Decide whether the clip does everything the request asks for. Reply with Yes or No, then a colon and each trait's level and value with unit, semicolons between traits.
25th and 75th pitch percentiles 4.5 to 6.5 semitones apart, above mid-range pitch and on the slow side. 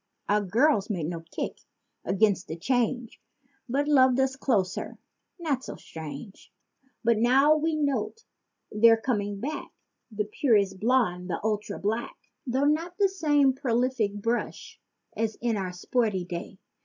Yes: average, 4.9 semitones; high, 230 Hz; slow, 130 wpm